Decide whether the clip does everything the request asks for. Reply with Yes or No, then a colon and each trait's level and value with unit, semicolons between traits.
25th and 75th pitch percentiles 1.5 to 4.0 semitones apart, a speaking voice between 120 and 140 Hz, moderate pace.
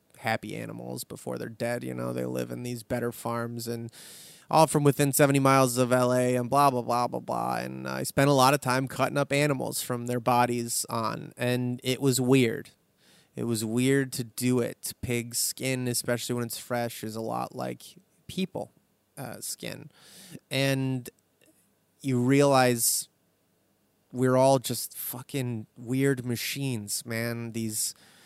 Yes: narrow, 2.4 semitones; low, 125 Hz; average, 160 wpm